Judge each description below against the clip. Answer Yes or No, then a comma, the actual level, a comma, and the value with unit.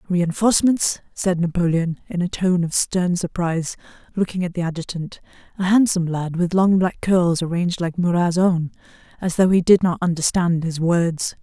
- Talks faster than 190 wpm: No, average, 160 wpm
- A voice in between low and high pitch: Yes, medium, 175 Hz